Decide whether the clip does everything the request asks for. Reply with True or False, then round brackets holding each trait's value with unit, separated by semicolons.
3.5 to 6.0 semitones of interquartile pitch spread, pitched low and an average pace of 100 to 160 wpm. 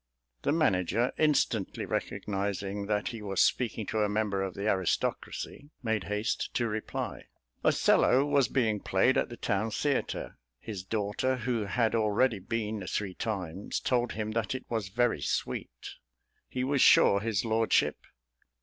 False (3.1 semitones; 110 Hz; 150 wpm)